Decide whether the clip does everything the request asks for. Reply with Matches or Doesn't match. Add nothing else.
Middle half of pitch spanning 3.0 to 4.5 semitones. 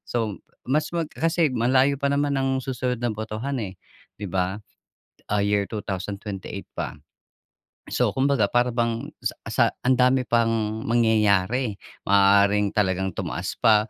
Matches